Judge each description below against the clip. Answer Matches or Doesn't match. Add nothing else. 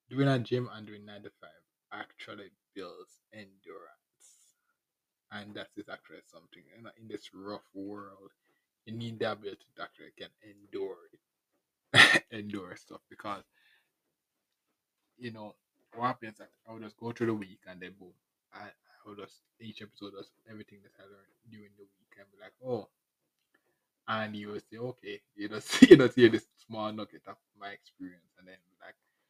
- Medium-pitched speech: Doesn't match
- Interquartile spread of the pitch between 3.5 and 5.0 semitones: Doesn't match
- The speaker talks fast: Doesn't match